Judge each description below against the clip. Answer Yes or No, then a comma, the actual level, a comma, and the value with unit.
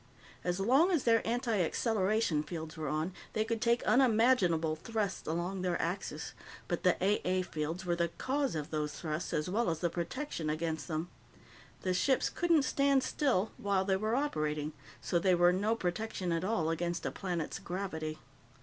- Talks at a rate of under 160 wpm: No, average, 175 wpm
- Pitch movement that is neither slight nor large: No, wide, 5.7 semitones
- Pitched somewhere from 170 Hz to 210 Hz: Yes, medium, 185 Hz